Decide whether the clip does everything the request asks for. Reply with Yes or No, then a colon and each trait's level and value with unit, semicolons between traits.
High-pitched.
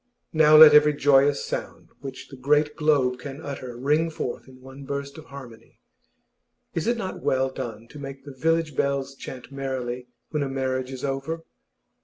No: medium, 140 Hz